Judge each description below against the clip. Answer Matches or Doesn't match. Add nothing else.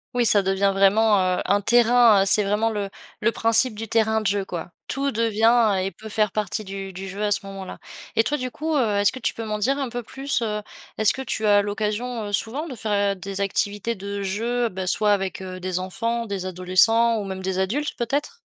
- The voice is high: Matches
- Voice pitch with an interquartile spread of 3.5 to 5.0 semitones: Doesn't match